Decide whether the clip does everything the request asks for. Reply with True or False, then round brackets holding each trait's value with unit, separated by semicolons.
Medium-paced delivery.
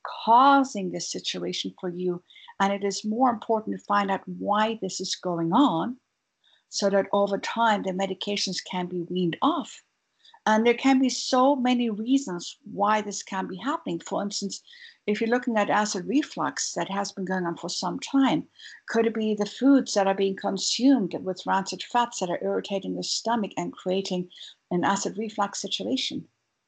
True (180 wpm)